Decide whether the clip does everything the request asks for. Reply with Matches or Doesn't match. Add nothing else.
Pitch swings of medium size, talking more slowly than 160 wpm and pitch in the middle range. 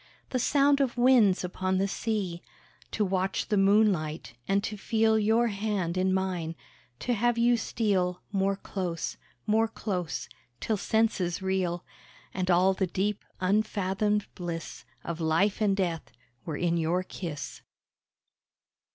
Doesn't match